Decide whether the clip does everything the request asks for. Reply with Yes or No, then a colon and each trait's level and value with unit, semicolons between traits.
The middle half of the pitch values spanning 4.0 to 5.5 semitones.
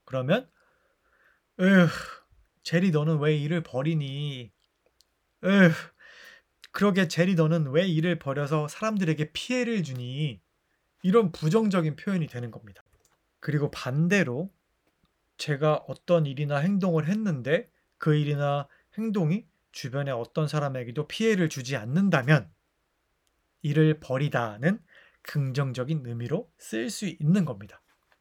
Yes: average, 4.4 semitones